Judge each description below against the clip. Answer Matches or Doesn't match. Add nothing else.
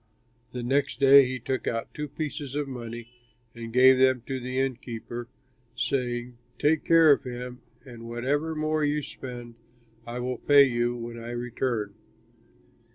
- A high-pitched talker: Doesn't match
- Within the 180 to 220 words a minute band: Doesn't match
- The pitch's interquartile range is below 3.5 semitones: Matches